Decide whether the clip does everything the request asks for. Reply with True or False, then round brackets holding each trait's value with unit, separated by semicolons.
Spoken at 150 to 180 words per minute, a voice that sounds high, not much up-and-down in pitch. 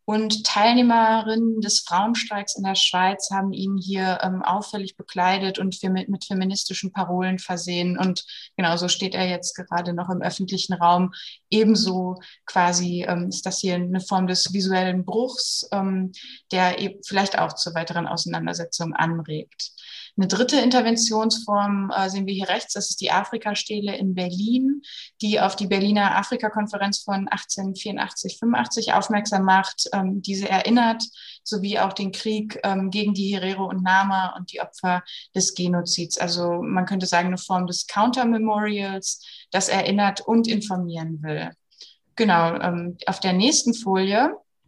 False (140 wpm; 195 Hz; 2.3 semitones)